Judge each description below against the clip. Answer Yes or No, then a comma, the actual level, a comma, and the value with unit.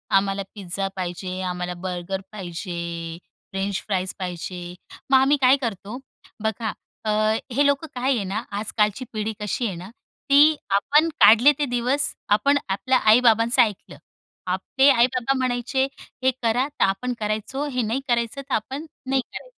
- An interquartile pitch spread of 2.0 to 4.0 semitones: No, average, 5.2 semitones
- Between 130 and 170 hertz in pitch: No, high, 225 Hz